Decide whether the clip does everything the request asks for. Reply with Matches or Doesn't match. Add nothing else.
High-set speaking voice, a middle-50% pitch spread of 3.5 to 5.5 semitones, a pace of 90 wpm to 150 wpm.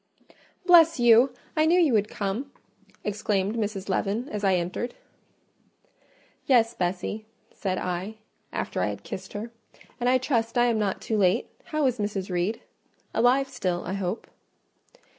Matches